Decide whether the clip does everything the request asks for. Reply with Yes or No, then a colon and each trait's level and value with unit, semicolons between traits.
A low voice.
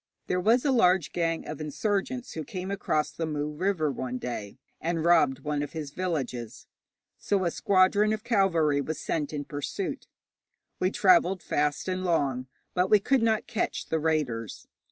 No: medium, 165 Hz